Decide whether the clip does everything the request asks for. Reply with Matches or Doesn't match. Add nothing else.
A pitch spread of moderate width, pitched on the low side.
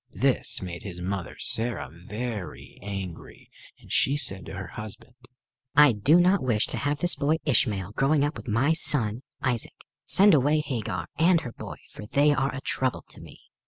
Doesn't match